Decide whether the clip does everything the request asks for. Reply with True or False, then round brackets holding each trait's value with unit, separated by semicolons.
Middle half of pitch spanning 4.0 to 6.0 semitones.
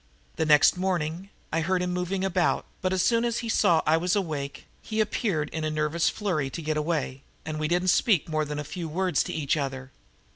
False (3.5 semitones)